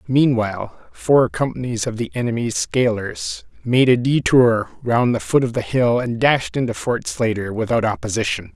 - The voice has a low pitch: Yes, low, 120 Hz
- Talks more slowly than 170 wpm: Yes, average, 160 wpm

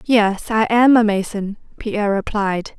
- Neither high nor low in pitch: No, high, 210 Hz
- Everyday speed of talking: Yes, average, 150 wpm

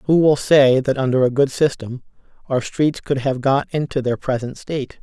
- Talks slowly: No, fast, 205 wpm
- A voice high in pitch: No, low, 135 Hz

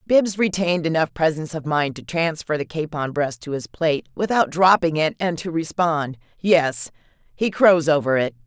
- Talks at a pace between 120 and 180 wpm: Yes, average, 170 wpm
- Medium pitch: Yes, medium, 160 Hz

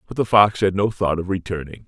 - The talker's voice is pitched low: Yes, very low, 95 Hz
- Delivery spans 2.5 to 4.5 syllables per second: No, 5.9 syllables/s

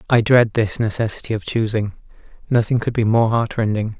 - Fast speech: No, average, 150 wpm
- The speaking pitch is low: Yes, low, 110 Hz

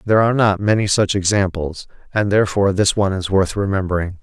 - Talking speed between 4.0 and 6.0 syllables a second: No, 6.4 syllables/s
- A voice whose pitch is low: Yes, very low, 95 Hz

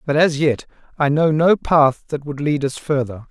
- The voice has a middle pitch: Yes, medium, 145 Hz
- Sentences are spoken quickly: Yes, fast, 220 wpm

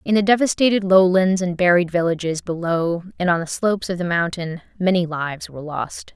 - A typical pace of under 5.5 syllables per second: No, 5.6 syllables/s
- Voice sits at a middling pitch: Yes, medium, 175 Hz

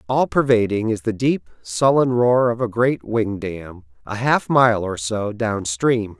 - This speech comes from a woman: No, male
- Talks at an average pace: Yes, average, 185 wpm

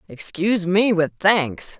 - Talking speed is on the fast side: No, slow, 135 wpm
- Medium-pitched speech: Yes, medium, 175 Hz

